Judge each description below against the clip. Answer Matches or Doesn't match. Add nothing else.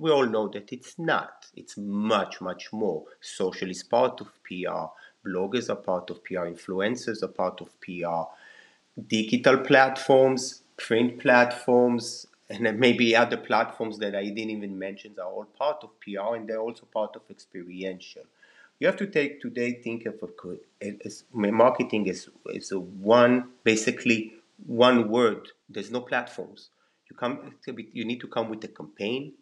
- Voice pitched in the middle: Doesn't match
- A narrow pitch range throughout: Doesn't match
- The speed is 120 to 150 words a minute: Doesn't match